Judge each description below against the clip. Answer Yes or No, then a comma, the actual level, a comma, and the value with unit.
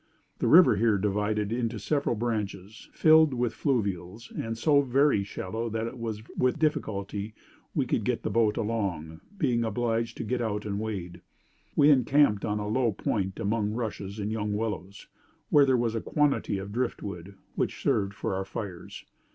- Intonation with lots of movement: No, average, 3.1 semitones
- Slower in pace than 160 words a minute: No, average, 170 wpm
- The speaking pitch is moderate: No, low, 110 Hz